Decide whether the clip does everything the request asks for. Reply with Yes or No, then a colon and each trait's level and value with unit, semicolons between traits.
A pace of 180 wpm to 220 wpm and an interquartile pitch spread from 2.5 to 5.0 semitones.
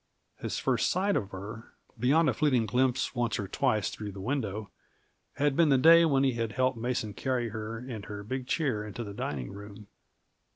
Yes: average, 195 wpm; average, 4.1 semitones